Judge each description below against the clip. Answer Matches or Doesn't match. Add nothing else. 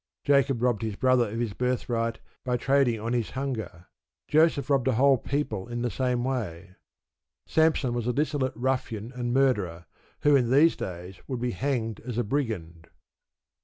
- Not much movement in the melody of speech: Doesn't match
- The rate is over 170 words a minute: Doesn't match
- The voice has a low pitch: Matches